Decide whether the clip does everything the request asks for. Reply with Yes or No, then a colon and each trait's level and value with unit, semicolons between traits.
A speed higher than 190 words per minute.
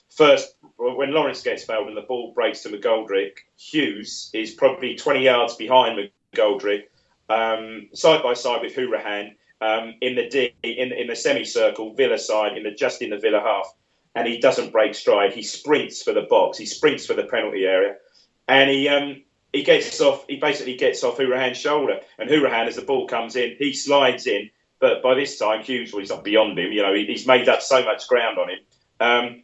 Yes: fast, 205 wpm